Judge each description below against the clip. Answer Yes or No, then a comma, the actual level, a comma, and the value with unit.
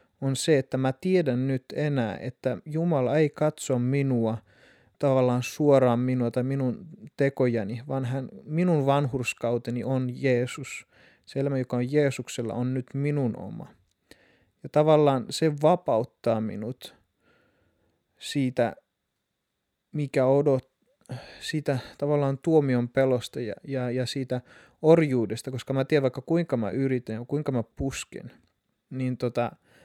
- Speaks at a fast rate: No, average, 125 wpm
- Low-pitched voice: Yes, low, 130 Hz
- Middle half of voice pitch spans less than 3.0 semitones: Yes, narrow, 2.4 semitones